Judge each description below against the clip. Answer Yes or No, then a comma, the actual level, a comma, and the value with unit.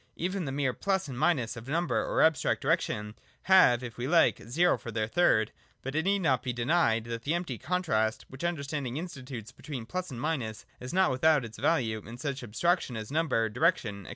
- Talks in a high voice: No, low, 135 Hz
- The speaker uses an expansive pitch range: Yes, wide, 6.3 semitones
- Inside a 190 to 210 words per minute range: Yes, fast, 205 wpm